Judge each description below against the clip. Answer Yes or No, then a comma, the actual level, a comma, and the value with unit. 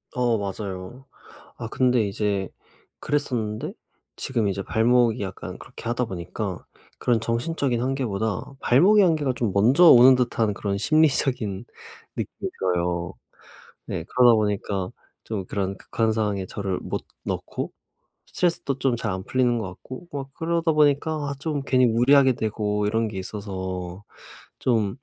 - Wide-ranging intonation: No, average, 4.8 semitones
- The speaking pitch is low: Yes, low, 115 Hz